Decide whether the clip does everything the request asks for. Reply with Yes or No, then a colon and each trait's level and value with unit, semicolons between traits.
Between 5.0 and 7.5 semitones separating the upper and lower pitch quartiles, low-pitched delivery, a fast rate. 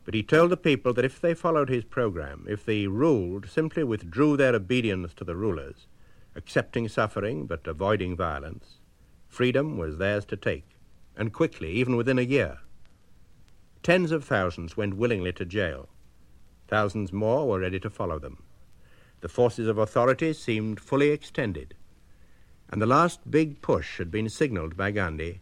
No: wide, 5.6 semitones; low, 110 Hz; average, 160 wpm